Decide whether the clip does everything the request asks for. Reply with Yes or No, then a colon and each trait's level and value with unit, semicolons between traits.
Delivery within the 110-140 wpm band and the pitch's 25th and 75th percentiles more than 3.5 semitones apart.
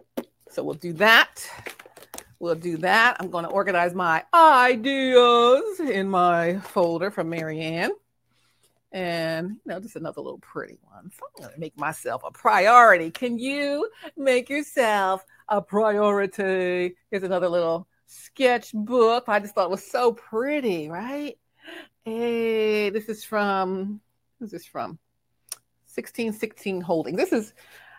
Yes: slow, 135 wpm; average, 5.3 semitones